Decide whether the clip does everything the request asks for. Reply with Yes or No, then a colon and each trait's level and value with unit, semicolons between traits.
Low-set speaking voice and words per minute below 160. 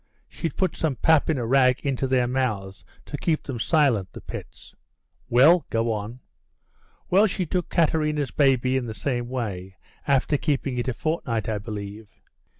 No: low, 130 Hz; average, 165 wpm